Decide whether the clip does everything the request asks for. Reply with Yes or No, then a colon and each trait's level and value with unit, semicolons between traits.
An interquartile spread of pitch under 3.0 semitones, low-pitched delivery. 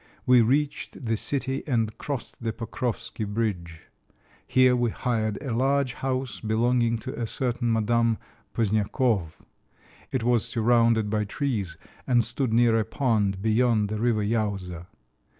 Yes: narrow, 2.6 semitones; low, 115 Hz